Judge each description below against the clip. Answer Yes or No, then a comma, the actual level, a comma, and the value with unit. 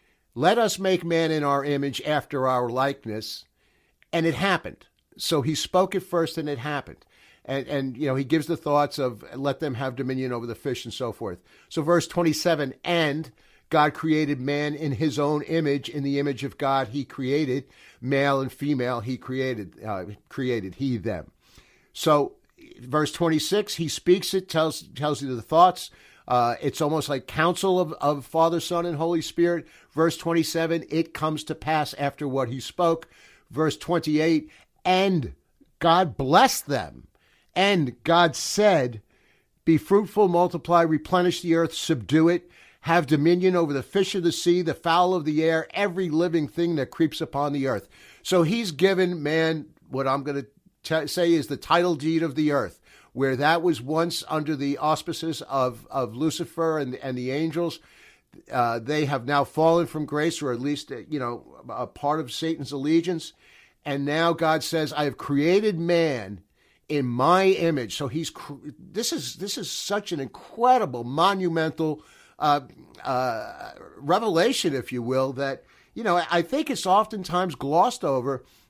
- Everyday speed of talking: Yes, average, 170 wpm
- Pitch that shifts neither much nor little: Yes, average, 3.5 semitones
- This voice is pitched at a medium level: Yes, medium, 155 Hz